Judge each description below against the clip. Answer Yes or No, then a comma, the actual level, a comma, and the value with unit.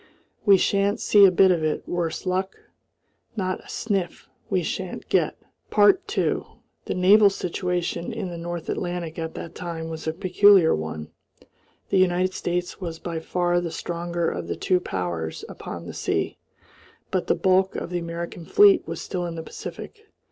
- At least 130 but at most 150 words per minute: No, average, 170 wpm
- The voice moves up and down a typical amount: No, narrow, 2.1 semitones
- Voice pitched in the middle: Yes, medium, 175 Hz